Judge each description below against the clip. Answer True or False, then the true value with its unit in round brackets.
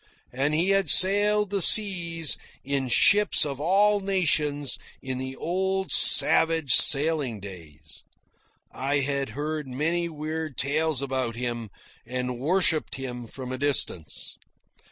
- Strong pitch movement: False (4.9 semitones)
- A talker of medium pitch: True (145 Hz)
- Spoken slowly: True (125 wpm)